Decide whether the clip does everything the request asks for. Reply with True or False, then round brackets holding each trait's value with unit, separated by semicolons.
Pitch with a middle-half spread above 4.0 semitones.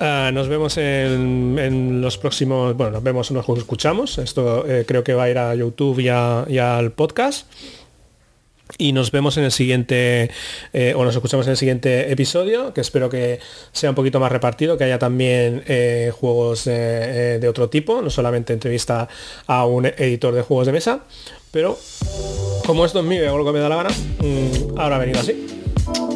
False (2.8 semitones)